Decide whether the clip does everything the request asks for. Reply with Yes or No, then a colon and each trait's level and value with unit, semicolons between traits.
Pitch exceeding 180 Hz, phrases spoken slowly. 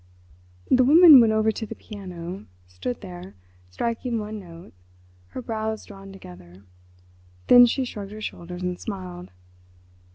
Yes: high, 190 Hz; slow, 120 wpm